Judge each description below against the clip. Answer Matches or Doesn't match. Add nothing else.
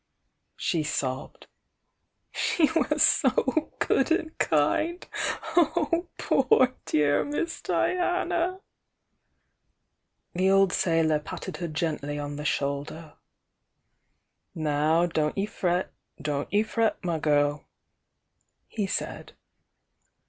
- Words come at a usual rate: Doesn't match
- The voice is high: Doesn't match